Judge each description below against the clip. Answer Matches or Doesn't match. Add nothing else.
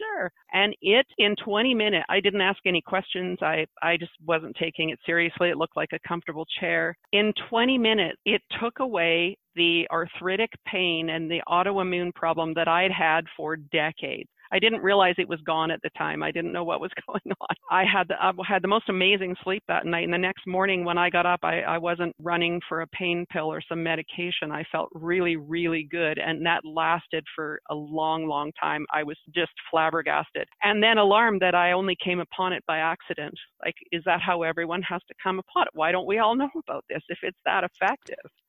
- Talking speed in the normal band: Doesn't match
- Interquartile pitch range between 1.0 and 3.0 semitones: Matches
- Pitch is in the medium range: Matches